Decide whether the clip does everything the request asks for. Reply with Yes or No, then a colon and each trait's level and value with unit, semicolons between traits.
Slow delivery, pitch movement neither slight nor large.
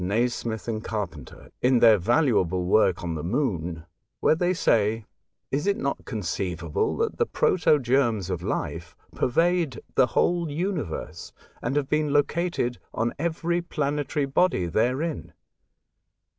No: slow, 130 wpm; wide, 7.3 semitones